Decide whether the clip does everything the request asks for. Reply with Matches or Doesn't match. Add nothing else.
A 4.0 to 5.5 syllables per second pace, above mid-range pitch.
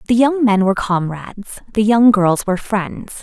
Matches